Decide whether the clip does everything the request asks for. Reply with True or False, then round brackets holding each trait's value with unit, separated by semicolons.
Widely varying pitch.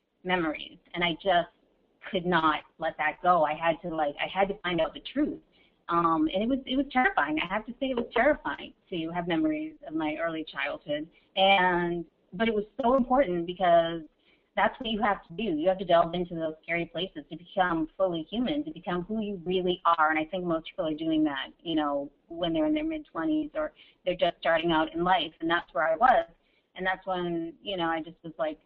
True (7.1 semitones)